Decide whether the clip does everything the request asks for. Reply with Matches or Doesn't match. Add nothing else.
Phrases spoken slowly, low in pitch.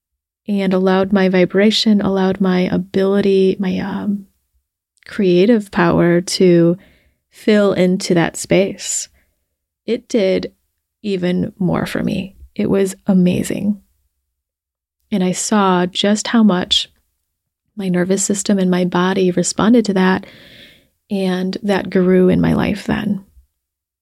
Doesn't match